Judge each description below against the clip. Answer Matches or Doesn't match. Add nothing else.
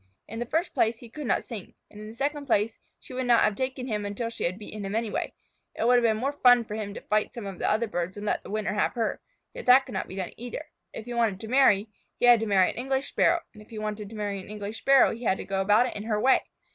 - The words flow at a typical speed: Doesn't match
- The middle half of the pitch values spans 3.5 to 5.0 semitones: Doesn't match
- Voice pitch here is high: Matches